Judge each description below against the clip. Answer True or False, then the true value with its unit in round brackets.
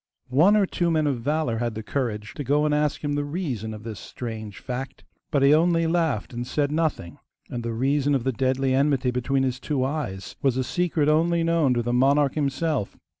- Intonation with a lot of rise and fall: False (3.8 semitones)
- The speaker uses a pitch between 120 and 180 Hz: True (135 Hz)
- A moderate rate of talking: False (215 wpm)